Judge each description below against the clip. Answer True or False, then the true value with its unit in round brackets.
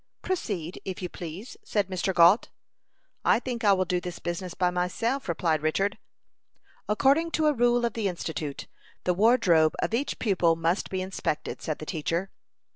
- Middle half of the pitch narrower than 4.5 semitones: False (5.1 semitones)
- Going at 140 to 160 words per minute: False (170 wpm)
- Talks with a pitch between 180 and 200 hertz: True (185 Hz)